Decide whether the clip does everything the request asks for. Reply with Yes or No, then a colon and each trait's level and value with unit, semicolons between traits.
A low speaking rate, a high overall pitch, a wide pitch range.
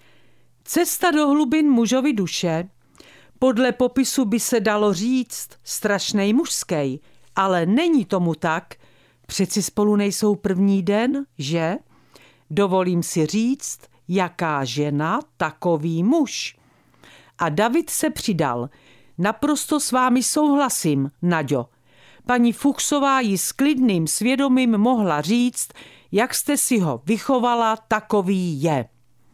Yes: slow, 110 wpm; high, 210 Hz; wide, 7.3 semitones